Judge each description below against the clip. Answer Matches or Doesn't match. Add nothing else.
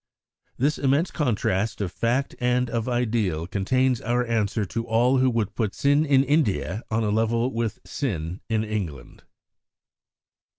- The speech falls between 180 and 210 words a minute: Doesn't match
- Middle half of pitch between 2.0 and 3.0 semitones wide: Doesn't match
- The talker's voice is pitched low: Matches